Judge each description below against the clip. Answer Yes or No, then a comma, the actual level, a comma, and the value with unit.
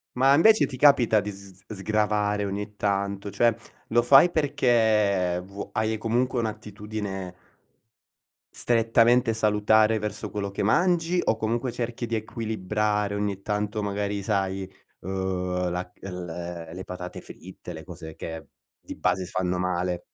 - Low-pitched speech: Yes, low, 105 Hz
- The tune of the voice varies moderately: Yes, average, 3.0 semitones